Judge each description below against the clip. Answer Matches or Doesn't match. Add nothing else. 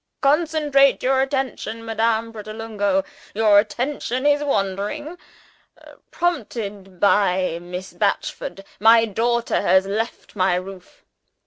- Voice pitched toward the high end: Matches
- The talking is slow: Matches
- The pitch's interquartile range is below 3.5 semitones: Doesn't match